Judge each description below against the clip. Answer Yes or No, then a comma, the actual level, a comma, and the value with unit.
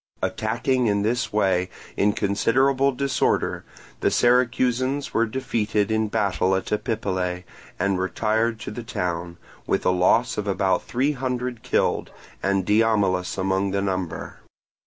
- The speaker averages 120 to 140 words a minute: Yes, slow, 135 wpm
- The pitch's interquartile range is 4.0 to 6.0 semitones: Yes, average, 4.4 semitones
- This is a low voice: Yes, low, 105 Hz